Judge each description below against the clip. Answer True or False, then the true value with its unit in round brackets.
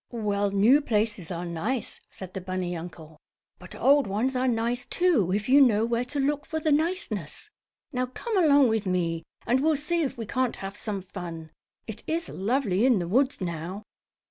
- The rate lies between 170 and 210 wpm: True (190 wpm)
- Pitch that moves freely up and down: True (6.6 semitones)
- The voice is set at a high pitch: True (225 Hz)